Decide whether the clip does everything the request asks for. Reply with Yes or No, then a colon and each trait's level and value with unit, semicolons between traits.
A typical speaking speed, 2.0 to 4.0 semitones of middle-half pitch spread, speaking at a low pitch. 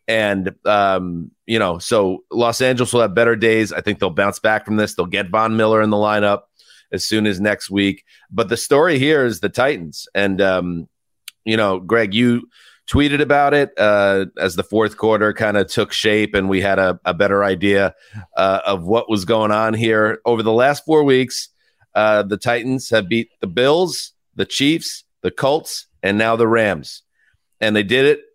Yes: average, 195 wpm; narrow, 2.5 semitones; low, 110 Hz